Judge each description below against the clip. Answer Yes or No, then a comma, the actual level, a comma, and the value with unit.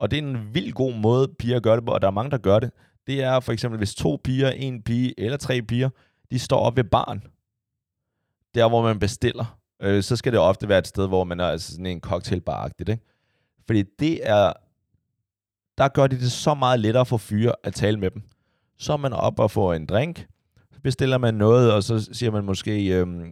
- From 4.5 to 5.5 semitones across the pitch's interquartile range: No, average, 3.7 semitones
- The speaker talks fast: Yes, fast, 230 wpm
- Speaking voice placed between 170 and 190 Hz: No, low, 115 Hz